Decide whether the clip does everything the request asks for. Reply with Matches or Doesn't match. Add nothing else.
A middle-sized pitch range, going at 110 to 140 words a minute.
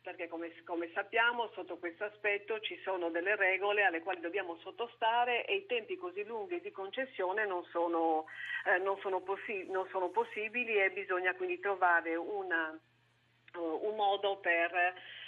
Doesn't match